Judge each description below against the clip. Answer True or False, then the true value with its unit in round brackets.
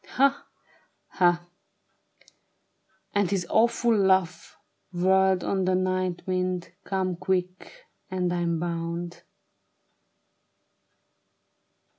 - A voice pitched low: False (185 Hz)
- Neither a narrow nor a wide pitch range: False (1.4 semitones)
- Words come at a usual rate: False (90 wpm)